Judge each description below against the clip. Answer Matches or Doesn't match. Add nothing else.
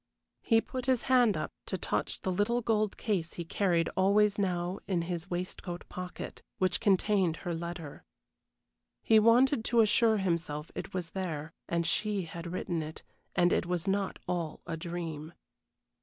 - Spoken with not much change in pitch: Doesn't match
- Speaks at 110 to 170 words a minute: Matches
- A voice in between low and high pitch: Matches